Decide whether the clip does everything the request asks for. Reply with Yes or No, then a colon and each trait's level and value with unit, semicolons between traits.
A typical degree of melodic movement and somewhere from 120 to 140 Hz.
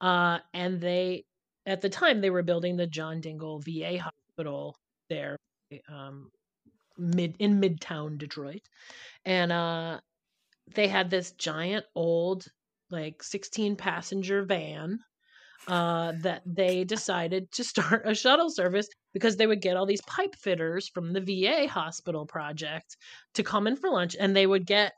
No: average, 3.0 semitones; medium, 185 Hz